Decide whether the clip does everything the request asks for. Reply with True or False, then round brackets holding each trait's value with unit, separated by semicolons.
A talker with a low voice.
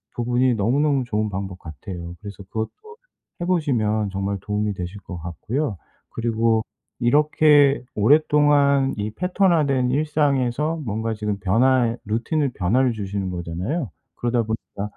True (115 Hz)